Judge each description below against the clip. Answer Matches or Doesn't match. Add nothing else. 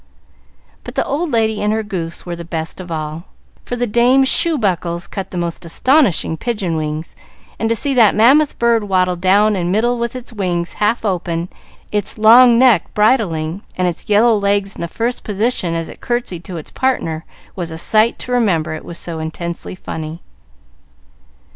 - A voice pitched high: Matches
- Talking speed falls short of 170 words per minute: Doesn't match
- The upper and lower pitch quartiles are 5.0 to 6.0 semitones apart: Matches